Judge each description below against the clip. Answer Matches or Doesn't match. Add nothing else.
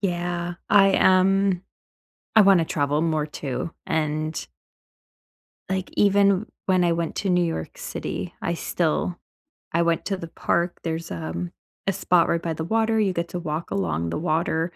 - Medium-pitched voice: Matches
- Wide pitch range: Doesn't match